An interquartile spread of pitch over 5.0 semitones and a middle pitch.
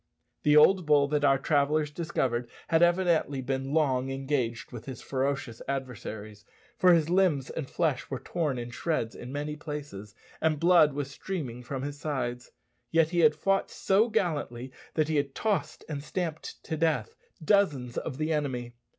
No: average, 3.5 semitones; medium, 145 Hz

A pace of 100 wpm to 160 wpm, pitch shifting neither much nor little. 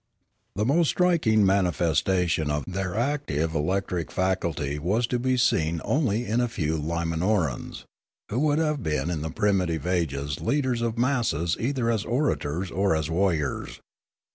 No: average, 150 wpm; wide, 6.7 semitones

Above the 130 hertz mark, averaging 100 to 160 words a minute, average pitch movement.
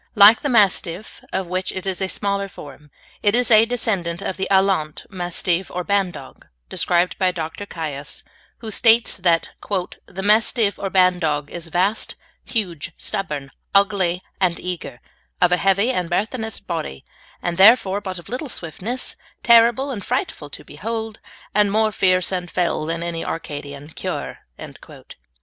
Yes: medium, 185 Hz; average, 150 wpm; average, 3.5 semitones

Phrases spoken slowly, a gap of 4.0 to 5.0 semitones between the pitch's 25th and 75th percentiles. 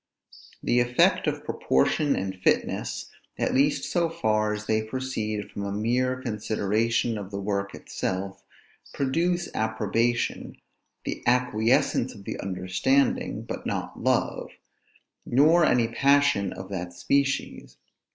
Yes: slow, 120 wpm; average, 4.6 semitones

